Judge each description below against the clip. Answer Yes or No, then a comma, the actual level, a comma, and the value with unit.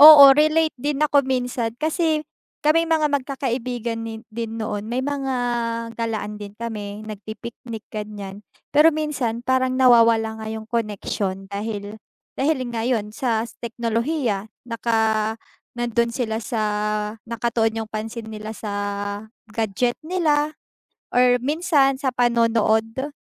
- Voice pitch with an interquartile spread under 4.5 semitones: Yes, average, 3.6 semitones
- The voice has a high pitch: Yes, high, 235 Hz